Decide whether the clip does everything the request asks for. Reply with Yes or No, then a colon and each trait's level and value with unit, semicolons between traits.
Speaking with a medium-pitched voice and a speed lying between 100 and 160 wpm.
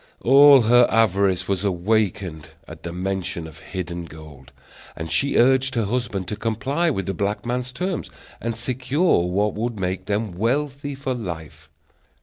No: low, 105 Hz; average, 155 wpm